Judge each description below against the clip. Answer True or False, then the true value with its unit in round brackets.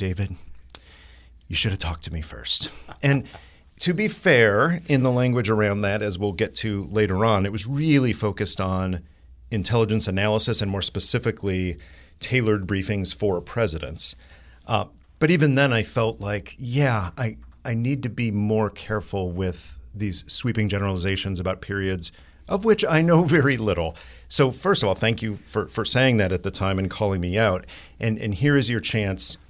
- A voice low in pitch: True (105 Hz)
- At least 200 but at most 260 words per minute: False (175 wpm)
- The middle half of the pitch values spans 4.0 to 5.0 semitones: True (4.3 semitones)